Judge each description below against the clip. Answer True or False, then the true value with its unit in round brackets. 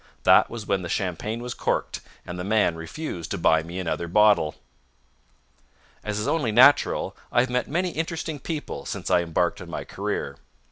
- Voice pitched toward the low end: True (105 Hz)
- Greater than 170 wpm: True (180 wpm)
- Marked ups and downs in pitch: True (6.8 semitones)